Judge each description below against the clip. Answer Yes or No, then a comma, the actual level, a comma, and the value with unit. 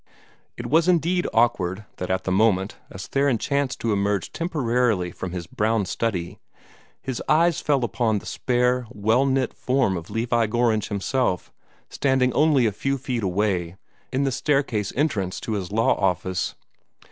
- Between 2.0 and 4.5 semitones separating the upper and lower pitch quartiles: No, average, 5.2 semitones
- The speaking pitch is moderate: No, low, 115 Hz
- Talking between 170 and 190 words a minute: No, average, 160 wpm